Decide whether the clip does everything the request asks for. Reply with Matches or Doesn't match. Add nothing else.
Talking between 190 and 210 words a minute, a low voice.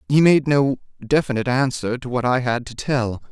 Matches